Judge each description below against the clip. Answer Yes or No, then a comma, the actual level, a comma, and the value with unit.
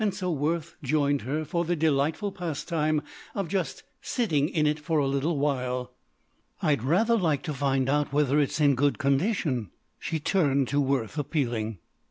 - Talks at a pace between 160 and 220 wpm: Yes, average, 165 wpm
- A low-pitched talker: No, medium, 150 Hz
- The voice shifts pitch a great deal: No, average, 3.1 semitones